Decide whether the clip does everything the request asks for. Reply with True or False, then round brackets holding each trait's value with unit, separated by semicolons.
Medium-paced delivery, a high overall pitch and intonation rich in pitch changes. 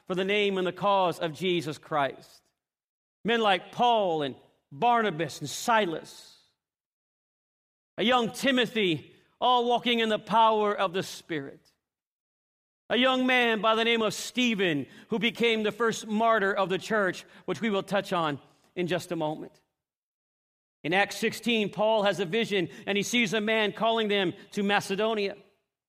False (160 wpm; 200 Hz; 4.2 semitones)